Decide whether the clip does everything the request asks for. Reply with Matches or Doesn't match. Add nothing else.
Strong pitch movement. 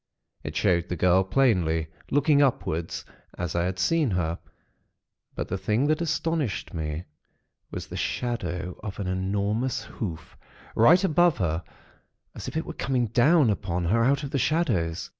Matches